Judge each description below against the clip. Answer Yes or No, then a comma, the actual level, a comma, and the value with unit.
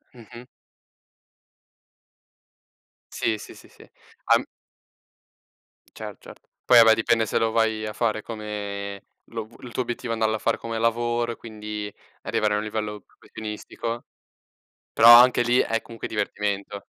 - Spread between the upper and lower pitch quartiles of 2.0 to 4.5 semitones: No, narrow, 1.6 semitones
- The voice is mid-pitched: No, low, 110 Hz